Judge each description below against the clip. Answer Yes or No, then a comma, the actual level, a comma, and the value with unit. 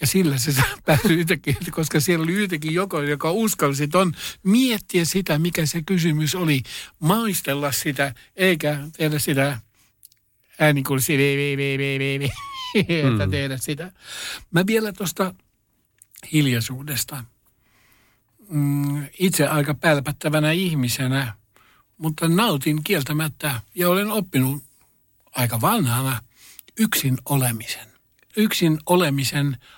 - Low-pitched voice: No, medium, 150 Hz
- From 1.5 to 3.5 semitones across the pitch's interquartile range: No, average, 4.3 semitones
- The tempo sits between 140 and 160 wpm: No, average, 100 wpm